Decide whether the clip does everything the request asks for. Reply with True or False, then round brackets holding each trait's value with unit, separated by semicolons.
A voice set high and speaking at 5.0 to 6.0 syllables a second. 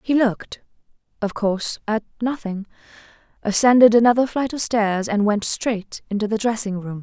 True (220 Hz; 5.1 syllables/s)